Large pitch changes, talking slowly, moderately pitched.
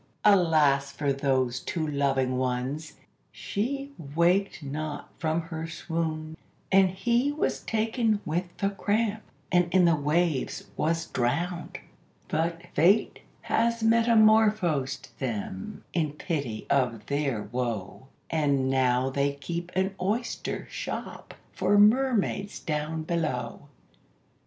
Yes: wide, 6.2 semitones; slow, 115 wpm; medium, 160 Hz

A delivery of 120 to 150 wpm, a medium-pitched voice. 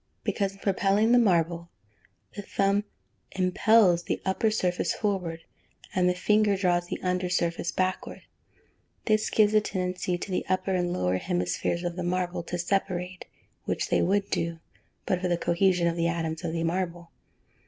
No: average, 170 wpm; medium, 180 Hz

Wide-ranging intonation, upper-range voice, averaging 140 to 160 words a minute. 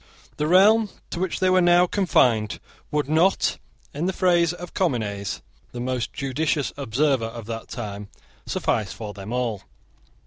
No: wide, 7.7 semitones; medium, 140 Hz; average, 150 wpm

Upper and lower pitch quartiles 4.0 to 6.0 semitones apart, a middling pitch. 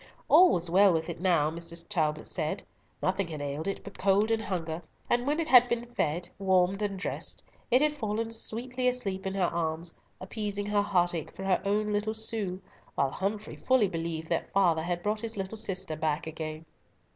No: average, 4.4 semitones; high, 195 Hz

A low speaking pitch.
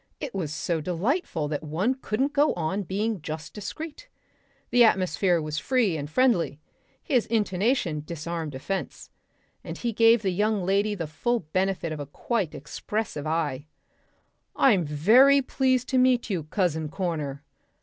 No: high, 190 Hz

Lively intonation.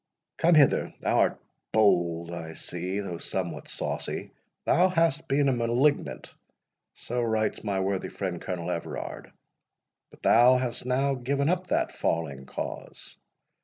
Yes: wide, 7.9 semitones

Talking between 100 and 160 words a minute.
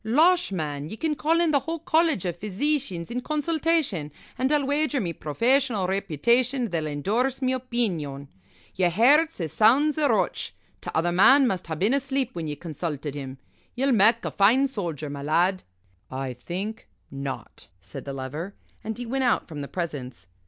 No: average, 175 wpm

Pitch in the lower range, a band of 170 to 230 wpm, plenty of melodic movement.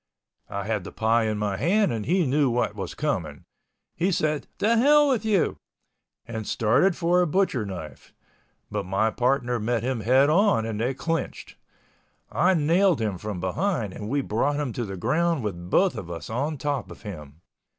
Yes: low, 125 Hz; average, 180 wpm; wide, 7.9 semitones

